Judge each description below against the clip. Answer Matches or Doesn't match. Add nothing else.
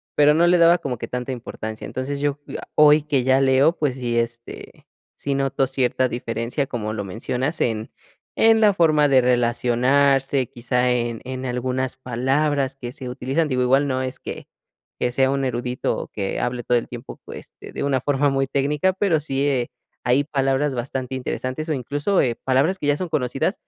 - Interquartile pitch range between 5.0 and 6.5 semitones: Doesn't match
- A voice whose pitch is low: Matches